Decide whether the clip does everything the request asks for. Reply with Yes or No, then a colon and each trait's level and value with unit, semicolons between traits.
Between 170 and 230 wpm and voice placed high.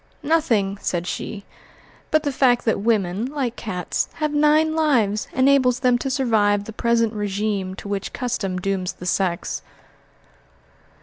No: average, 140 wpm; high, 225 Hz